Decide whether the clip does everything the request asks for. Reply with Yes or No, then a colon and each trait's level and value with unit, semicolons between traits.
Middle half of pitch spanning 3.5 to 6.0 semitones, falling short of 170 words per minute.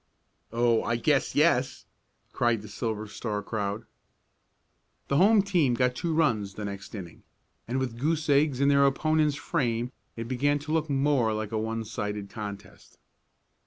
Yes: average, 5.0 semitones; average, 160 wpm